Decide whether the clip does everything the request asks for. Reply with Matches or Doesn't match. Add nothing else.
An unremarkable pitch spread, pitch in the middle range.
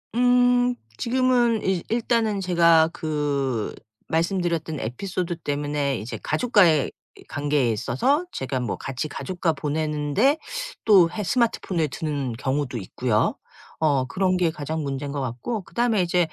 Doesn't match